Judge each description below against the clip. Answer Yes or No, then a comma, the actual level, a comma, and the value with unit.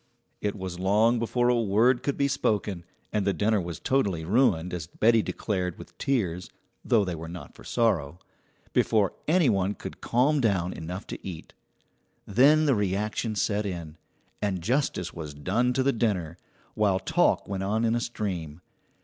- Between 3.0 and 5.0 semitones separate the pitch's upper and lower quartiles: Yes, average, 4.7 semitones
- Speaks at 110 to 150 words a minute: No, average, 170 wpm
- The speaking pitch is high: No, low, 100 Hz